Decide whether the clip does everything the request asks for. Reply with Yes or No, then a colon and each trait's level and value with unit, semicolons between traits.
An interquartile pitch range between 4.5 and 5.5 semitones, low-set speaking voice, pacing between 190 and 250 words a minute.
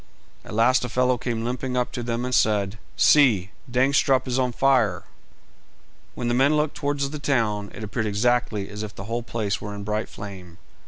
No: average, 3.5 semitones; low, 120 Hz; average, 200 wpm